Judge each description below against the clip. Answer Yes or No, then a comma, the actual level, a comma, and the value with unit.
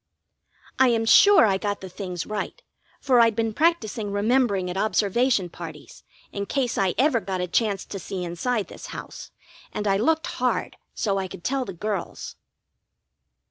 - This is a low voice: No, high, 210 Hz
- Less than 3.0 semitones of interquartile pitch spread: No, average, 4.1 semitones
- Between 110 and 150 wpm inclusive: No, average, 170 wpm